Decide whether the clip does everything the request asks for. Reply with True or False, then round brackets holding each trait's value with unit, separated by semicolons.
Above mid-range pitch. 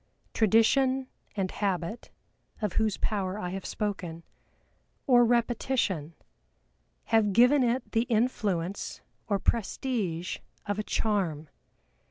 True (210 Hz)